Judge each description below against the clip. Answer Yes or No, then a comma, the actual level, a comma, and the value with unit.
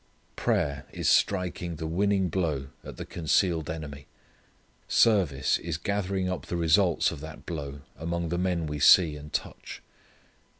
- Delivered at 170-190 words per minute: No, average, 145 wpm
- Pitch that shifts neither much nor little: Yes, average, 3.5 semitones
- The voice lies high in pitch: No, very low, 85 Hz